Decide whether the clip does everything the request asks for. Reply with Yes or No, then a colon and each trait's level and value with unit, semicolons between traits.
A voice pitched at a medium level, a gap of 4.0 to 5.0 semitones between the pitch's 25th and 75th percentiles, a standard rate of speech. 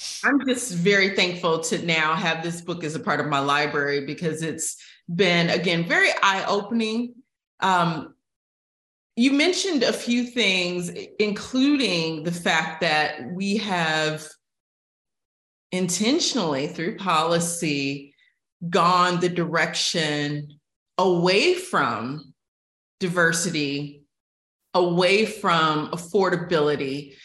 No: medium, 175 Hz; average, 4.3 semitones; slow, 100 wpm